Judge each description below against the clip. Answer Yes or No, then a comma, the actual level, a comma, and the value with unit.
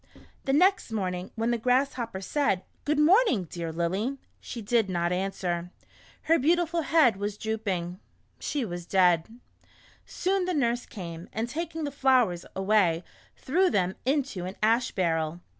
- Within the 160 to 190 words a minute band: No, average, 150 wpm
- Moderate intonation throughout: No, wide, 7.5 semitones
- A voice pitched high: Yes, high, 220 Hz